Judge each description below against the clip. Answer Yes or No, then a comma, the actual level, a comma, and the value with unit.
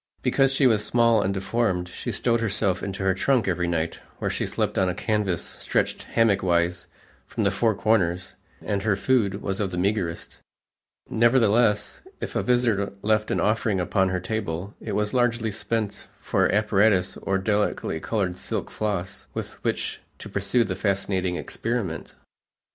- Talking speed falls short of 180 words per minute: Yes, average, 165 wpm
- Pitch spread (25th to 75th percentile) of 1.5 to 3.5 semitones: Yes, average, 3.1 semitones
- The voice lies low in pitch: Yes, low, 100 Hz